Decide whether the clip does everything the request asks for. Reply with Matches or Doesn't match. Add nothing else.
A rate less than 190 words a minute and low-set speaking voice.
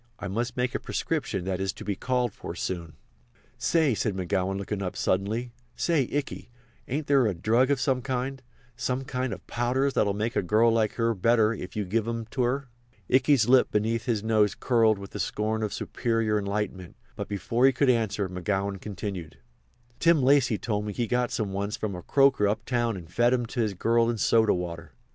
Doesn't match